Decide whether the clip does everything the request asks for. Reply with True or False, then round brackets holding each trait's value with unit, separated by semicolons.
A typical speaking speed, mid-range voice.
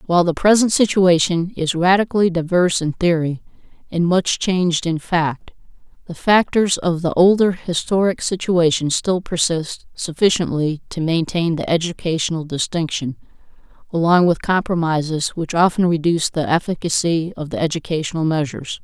False (130 wpm; 170 Hz)